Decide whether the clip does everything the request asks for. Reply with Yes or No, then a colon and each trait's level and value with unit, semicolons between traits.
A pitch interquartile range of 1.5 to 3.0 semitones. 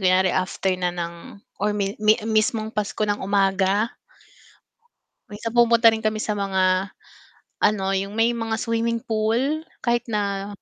Yes: narrow, 2.6 semitones